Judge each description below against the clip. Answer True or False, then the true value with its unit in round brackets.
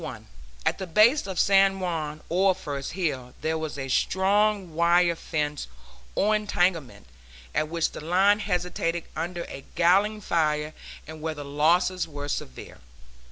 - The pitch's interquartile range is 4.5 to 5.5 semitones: False (3.8 semitones)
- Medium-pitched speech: True (170 Hz)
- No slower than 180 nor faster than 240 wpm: False (145 wpm)